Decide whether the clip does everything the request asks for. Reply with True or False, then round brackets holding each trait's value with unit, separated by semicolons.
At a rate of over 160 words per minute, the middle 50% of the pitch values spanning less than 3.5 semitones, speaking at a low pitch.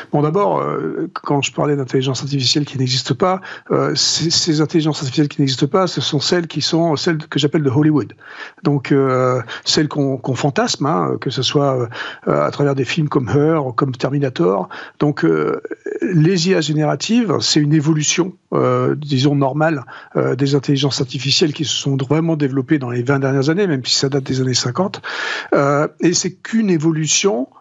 False (185 wpm; 3.1 semitones; 150 Hz)